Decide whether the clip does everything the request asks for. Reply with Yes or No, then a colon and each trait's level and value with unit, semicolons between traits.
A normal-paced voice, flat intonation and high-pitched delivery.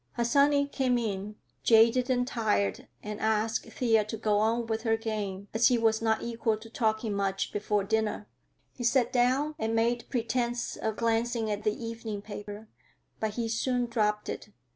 Yes: average, 170 wpm; narrow, 2.0 semitones; high, 225 Hz